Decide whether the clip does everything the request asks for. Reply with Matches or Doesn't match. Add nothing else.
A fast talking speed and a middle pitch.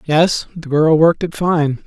Doesn't match